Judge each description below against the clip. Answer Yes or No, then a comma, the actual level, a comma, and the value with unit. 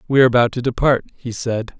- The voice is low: Yes, low, 120 Hz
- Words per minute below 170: No, average, 200 wpm